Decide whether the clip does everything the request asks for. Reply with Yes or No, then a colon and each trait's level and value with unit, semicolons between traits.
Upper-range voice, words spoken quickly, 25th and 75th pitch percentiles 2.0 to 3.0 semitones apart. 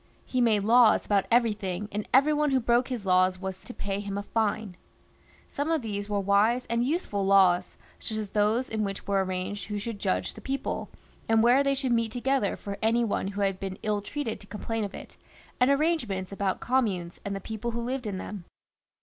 No: high, 210 Hz; fast, 210 wpm; average, 3.5 semitones